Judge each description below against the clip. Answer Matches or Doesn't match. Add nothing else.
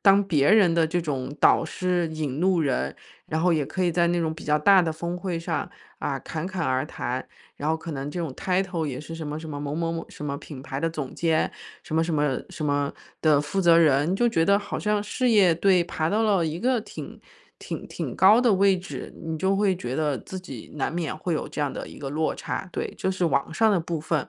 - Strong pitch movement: Doesn't match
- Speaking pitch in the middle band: Matches